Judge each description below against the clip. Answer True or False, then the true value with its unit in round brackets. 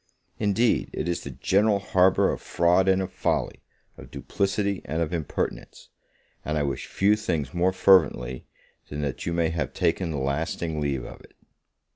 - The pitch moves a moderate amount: True (4.3 semitones)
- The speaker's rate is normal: True (170 wpm)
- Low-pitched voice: True (85 Hz)